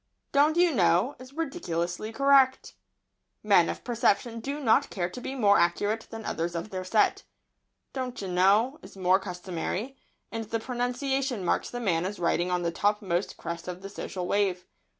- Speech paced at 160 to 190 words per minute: Yes, average, 170 wpm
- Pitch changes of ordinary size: No, wide, 5.8 semitones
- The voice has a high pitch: Yes, high, 205 Hz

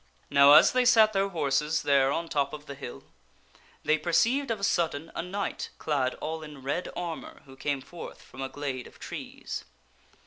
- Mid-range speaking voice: Yes, medium, 150 Hz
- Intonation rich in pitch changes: No, average, 4.1 semitones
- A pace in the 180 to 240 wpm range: Yes, average, 185 wpm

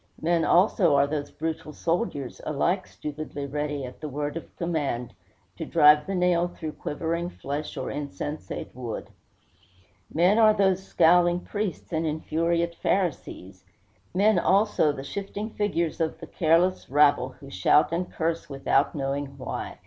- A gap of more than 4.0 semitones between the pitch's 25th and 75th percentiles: No, average, 3.5 semitones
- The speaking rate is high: No, average, 145 wpm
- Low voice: No, medium, 160 Hz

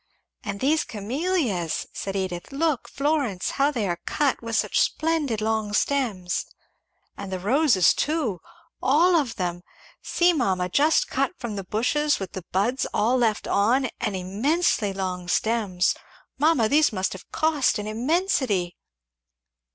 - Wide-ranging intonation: Yes, wide, 7.2 semitones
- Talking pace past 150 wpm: No, average, 145 wpm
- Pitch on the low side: No, high, 230 Hz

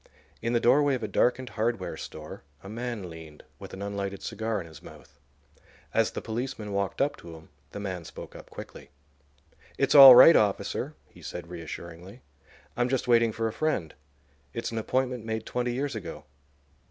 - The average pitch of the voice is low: Yes, low, 110 Hz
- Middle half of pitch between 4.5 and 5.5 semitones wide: Yes, average, 4.9 semitones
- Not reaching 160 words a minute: No, average, 175 wpm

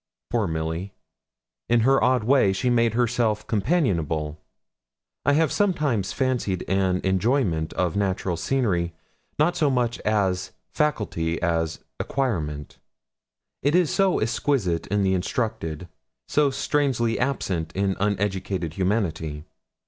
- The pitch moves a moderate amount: No, wide, 6.7 semitones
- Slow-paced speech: Yes, slow, 120 wpm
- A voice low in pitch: Yes, low, 105 Hz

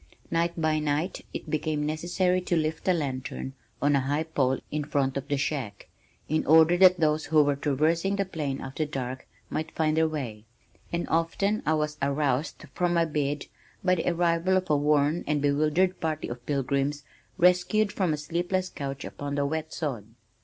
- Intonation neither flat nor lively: Yes, average, 3.0 semitones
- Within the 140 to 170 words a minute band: No, average, 180 wpm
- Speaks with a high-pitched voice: No, medium, 155 Hz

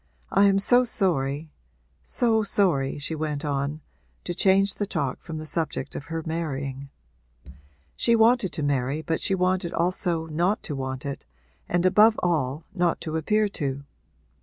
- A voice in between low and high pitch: Yes, medium, 165 Hz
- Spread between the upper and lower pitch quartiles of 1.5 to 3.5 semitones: No, average, 5.1 semitones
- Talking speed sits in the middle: Yes, average, 160 wpm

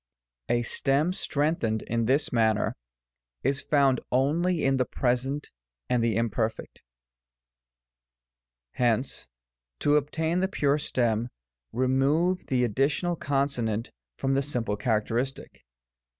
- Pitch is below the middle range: Yes, low, 130 Hz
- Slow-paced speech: Yes, slow, 105 wpm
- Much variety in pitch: No, average, 3.8 semitones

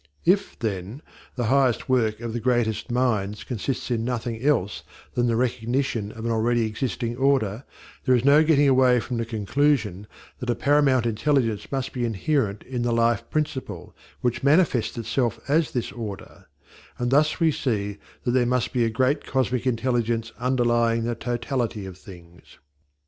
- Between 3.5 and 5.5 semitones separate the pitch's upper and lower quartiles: No, average, 2.7 semitones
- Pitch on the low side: Yes, low, 120 Hz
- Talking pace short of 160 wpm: No, average, 165 wpm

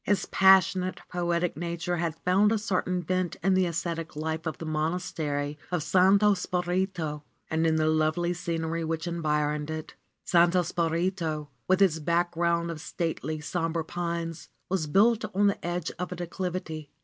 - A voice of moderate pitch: Yes, medium, 170 Hz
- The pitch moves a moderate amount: No, narrow, 2.2 semitones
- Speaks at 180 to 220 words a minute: No, average, 155 wpm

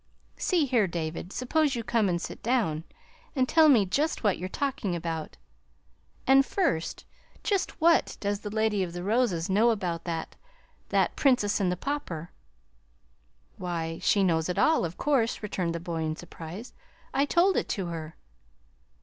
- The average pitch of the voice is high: Yes, high, 200 Hz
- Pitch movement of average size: No, wide, 7.1 semitones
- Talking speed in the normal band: Yes, average, 165 wpm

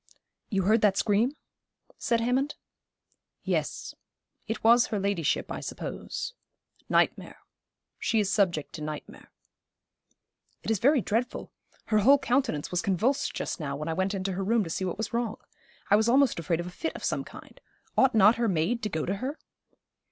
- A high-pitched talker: Yes, high, 210 Hz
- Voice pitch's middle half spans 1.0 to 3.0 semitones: No, average, 4.3 semitones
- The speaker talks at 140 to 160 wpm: No, average, 175 wpm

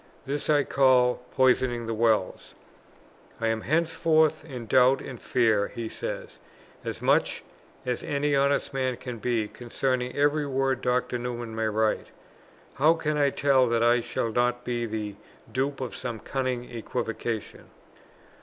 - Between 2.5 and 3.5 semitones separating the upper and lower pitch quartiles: Yes, average, 2.8 semitones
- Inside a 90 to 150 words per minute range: Yes, average, 145 wpm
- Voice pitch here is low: Yes, low, 125 Hz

